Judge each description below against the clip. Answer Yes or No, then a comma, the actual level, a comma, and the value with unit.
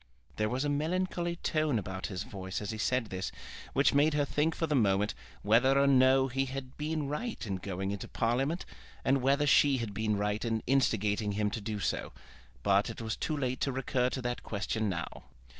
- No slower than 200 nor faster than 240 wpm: Yes, fast, 205 wpm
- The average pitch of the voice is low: Yes, low, 125 Hz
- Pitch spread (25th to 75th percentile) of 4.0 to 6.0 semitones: Yes, average, 5.2 semitones